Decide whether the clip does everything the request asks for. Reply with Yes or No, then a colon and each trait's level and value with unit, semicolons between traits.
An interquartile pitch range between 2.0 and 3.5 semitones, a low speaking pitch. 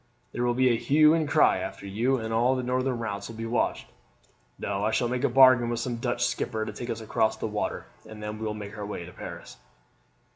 Yes: average, 2.7 semitones; low, 115 Hz